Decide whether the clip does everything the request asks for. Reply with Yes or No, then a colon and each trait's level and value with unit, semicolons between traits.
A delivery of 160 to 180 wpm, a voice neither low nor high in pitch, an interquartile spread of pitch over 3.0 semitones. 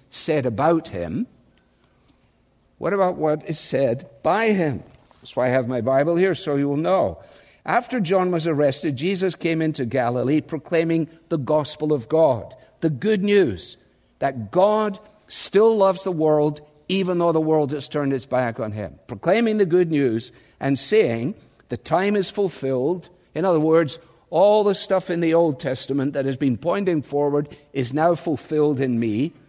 Yes: average, 170 wpm; medium, 155 Hz; average, 4.9 semitones